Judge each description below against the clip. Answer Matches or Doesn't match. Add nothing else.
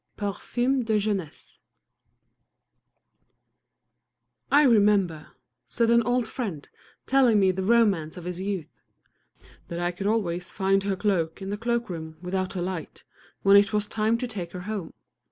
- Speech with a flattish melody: Doesn't match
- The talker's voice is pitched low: Doesn't match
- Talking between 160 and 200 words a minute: Doesn't match